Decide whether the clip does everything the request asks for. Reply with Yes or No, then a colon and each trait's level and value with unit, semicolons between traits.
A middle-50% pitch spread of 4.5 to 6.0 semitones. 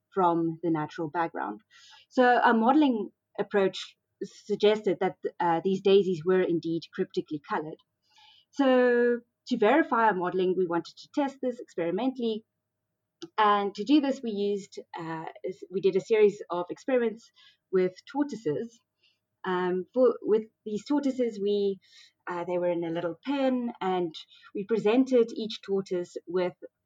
Yes: wide, 5.6 semitones